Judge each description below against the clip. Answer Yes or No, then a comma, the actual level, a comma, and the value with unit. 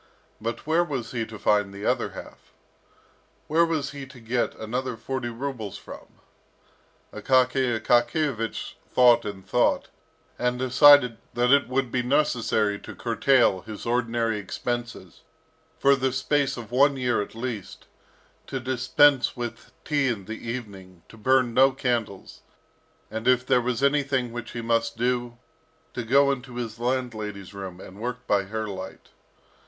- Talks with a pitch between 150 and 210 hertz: No, low, 120 Hz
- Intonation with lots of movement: No, average, 2.7 semitones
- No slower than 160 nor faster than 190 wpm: No, average, 150 wpm